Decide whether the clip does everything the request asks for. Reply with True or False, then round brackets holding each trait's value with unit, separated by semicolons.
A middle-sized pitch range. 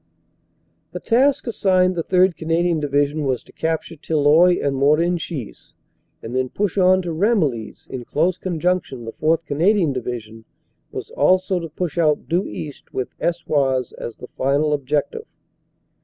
True (4.6 semitones)